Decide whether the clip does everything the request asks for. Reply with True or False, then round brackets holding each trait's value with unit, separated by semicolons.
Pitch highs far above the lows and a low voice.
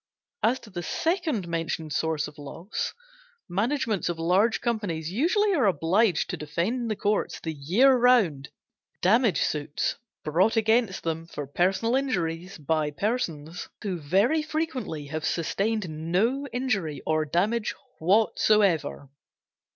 False (6.4 semitones; 190 Hz)